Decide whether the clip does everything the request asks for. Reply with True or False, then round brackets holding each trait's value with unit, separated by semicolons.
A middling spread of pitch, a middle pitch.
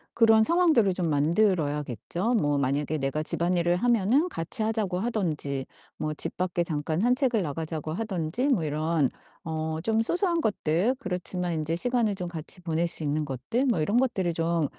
False (6.2 semitones; 175 Hz)